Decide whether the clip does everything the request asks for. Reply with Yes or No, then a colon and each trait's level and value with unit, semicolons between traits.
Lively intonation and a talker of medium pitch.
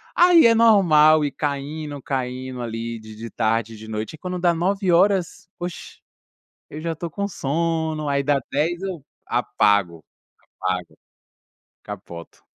Yes: wide, 7.0 semitones; medium, 150 Hz